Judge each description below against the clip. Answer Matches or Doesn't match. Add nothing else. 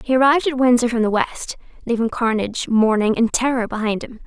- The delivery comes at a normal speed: Matches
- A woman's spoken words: Matches